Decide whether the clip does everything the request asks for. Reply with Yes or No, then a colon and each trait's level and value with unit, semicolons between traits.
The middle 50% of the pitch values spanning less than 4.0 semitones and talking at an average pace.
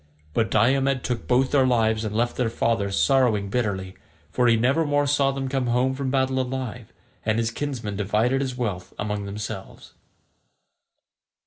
Yes: average, 3.6 semitones; average, 155 wpm